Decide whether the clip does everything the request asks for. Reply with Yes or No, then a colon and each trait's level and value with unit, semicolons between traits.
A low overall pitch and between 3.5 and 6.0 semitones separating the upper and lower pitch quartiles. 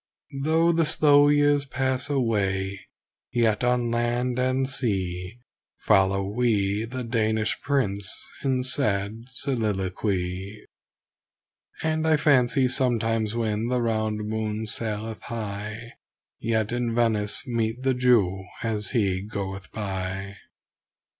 Yes: low, 115 Hz; average, 3.8 semitones